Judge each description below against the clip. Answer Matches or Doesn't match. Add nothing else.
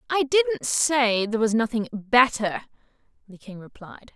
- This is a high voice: Matches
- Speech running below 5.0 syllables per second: Matches